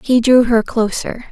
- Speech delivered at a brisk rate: No, average, 185 wpm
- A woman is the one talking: Yes, female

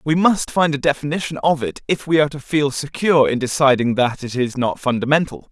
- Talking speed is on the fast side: Yes, fast, 220 wpm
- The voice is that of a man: Yes, male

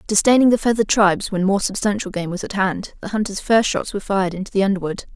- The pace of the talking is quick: Yes, fast, 235 wpm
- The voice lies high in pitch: Yes, high, 200 Hz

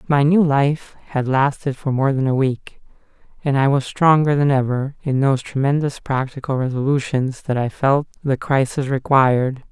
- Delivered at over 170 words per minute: No, average, 165 wpm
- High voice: No, low, 135 Hz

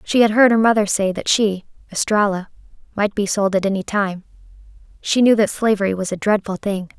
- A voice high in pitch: Yes, high, 205 Hz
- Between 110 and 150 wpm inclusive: No, average, 190 wpm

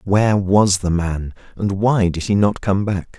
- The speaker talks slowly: No, fast, 205 wpm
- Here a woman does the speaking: No, male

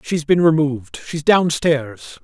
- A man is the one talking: Yes, male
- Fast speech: No, slow, 135 wpm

